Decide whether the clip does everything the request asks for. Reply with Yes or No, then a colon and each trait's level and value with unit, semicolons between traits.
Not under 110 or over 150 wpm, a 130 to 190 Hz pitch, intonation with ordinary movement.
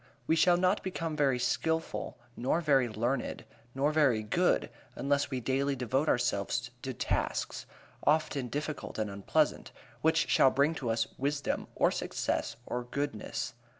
Yes: average, 145 wpm; medium, 140 Hz; average, 3.9 semitones